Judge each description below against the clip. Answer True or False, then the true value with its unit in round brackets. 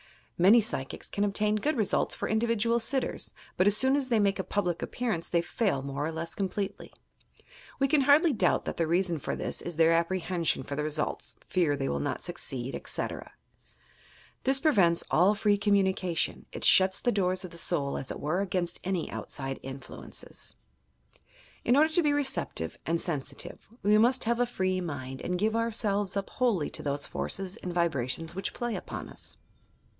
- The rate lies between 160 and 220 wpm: True (190 wpm)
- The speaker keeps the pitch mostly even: False (5.1 semitones)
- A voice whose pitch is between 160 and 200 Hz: True (190 Hz)